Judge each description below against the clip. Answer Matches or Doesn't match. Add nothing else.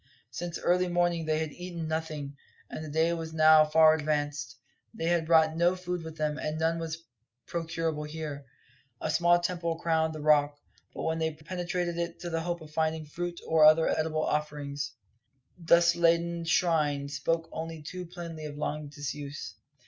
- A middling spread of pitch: Doesn't match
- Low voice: Doesn't match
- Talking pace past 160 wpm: Matches